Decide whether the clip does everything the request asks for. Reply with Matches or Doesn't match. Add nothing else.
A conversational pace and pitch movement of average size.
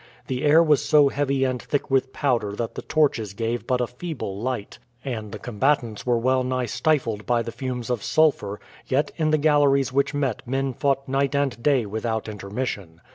Matches